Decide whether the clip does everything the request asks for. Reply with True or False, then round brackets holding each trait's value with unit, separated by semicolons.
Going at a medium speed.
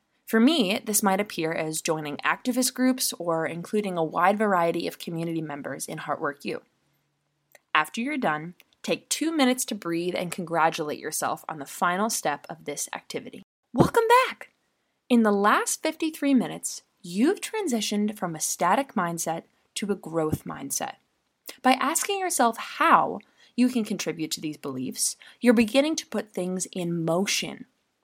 True (155 wpm)